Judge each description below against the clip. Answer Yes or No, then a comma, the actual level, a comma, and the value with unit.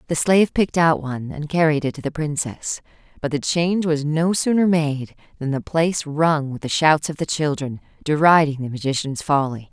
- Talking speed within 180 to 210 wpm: Yes, average, 200 wpm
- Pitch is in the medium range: Yes, medium, 150 Hz